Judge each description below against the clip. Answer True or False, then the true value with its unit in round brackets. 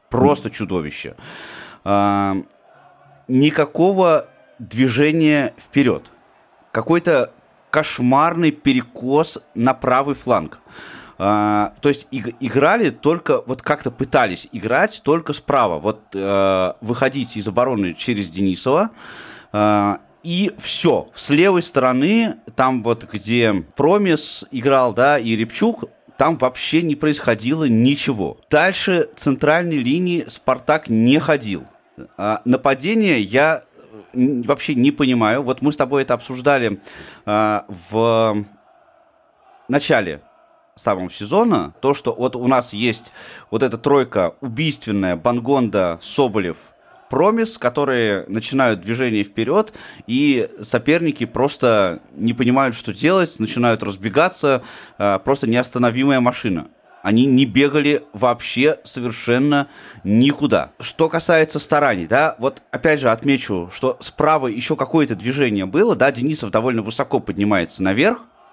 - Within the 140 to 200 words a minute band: False (110 wpm)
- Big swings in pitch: False (4.8 semitones)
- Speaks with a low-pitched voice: True (130 Hz)